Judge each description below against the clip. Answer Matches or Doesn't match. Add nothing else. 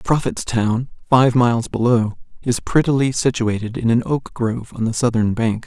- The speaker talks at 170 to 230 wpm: Doesn't match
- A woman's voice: Doesn't match